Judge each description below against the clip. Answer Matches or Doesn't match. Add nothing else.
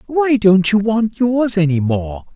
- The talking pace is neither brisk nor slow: Matches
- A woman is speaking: Doesn't match